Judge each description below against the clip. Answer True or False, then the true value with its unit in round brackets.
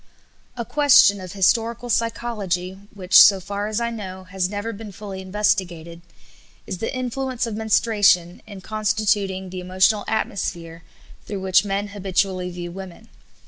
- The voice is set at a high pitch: True (200 Hz)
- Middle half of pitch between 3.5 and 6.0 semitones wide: False (2.9 semitones)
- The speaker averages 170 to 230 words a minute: False (145 wpm)